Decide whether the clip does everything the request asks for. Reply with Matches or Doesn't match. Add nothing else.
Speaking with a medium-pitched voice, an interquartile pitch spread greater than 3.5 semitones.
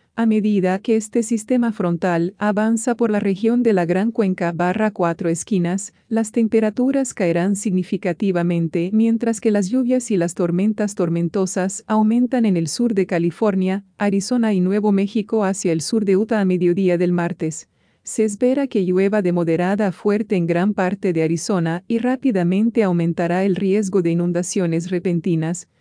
Doesn't match